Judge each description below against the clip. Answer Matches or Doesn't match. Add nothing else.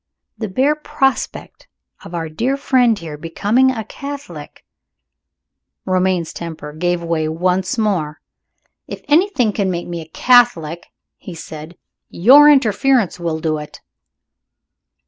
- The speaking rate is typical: Doesn't match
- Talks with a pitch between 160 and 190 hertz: Matches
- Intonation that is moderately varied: Doesn't match